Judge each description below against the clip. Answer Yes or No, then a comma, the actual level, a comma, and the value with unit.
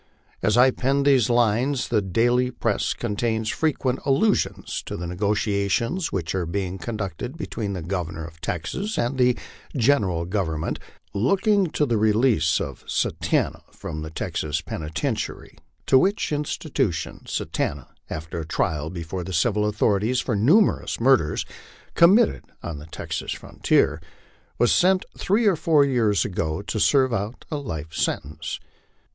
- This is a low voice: Yes, low, 110 Hz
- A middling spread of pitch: No, wide, 7.5 semitones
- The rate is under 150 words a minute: Yes, average, 140 wpm